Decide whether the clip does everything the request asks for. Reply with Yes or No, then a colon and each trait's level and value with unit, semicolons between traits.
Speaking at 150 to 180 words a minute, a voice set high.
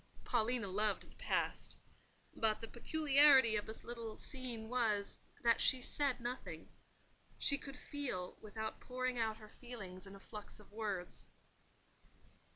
No: average, 140 wpm; high, 225 Hz